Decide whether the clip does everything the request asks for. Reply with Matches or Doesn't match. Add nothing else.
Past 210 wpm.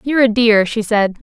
Matches